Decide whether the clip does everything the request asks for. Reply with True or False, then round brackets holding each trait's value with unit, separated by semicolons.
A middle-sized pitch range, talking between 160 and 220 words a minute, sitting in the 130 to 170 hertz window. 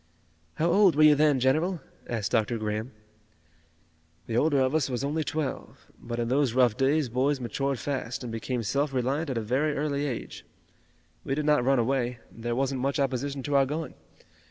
True (3.2 semitones; 190 wpm; 135 Hz)